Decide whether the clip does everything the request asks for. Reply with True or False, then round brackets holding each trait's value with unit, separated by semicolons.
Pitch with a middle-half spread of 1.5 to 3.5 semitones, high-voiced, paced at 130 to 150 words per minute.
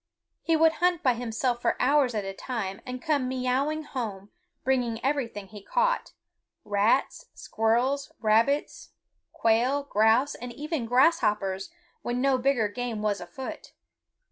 False (4.2 semitones; 245 Hz; 135 wpm)